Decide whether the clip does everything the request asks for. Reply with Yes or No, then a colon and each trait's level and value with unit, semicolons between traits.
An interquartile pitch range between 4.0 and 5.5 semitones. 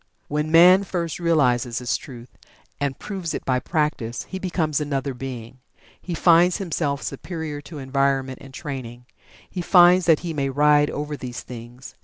Yes: average, 4.3 semitones